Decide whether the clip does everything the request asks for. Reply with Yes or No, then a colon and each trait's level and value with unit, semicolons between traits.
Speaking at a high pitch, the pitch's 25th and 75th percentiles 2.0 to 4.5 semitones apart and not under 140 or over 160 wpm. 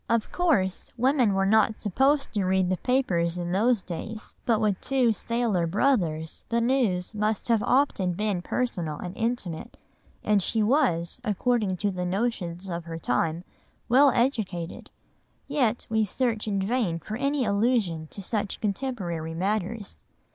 No: high, 210 Hz; average, 5.0 semitones; average, 150 wpm